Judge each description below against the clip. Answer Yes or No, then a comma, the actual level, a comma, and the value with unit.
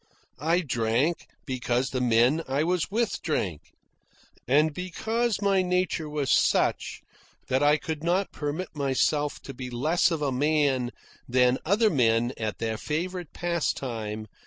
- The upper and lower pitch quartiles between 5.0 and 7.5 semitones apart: Yes, wide, 5.5 semitones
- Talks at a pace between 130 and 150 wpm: Yes, average, 140 wpm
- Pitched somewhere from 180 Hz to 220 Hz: No, medium, 145 Hz